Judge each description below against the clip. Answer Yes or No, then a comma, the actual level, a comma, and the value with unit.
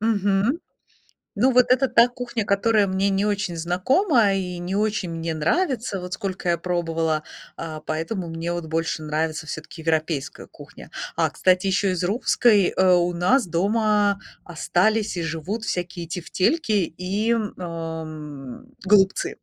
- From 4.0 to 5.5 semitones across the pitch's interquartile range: Yes, average, 4.4 semitones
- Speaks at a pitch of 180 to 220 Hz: Yes, medium, 185 Hz